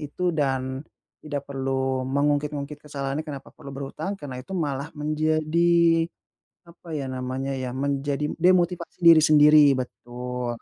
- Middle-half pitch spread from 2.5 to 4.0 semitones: Yes, average, 2.9 semitones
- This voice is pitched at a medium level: Yes, medium, 145 Hz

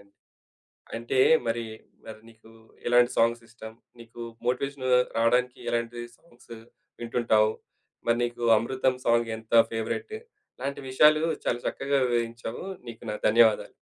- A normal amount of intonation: No, narrow, 1.6 semitones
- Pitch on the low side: Yes, low, 120 Hz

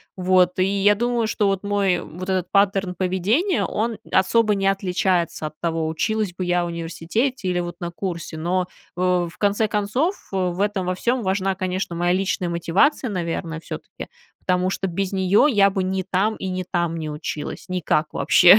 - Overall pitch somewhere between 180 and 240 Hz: Yes, medium, 185 Hz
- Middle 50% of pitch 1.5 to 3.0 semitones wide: Yes, narrow, 2.4 semitones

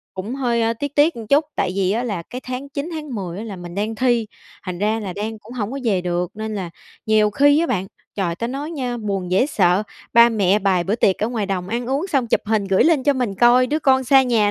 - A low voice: No, high, 225 Hz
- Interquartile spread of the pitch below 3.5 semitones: No, average, 4.7 semitones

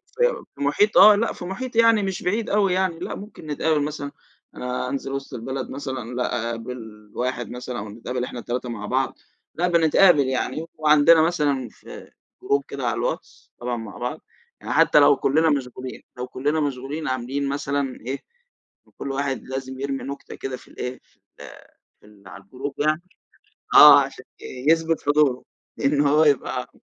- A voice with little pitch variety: No, average, 4.1 semitones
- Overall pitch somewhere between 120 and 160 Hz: Yes, medium, 140 Hz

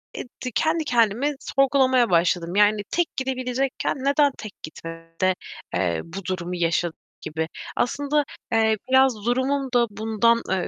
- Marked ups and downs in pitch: Yes, wide, 6.7 semitones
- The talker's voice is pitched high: Yes, high, 230 Hz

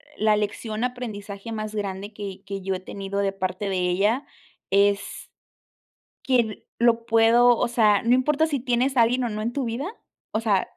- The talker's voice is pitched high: Yes, high, 215 Hz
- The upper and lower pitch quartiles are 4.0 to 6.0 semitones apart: No, average, 3.1 semitones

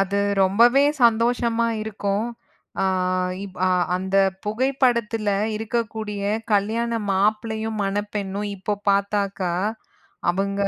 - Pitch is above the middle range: Yes, high, 210 Hz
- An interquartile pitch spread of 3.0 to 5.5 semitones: No, narrow, 2.5 semitones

